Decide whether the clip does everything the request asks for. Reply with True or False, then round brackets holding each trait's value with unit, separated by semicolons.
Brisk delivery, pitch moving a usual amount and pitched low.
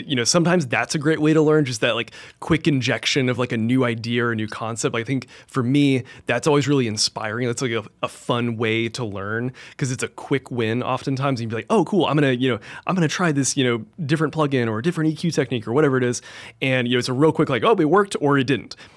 True (270 wpm; 4.3 semitones; 130 Hz)